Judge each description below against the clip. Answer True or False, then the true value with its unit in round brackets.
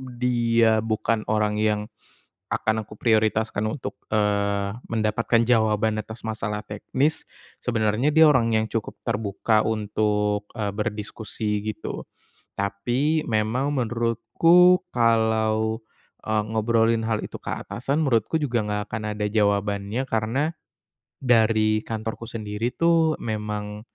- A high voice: False (110 Hz)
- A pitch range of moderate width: False (1.9 semitones)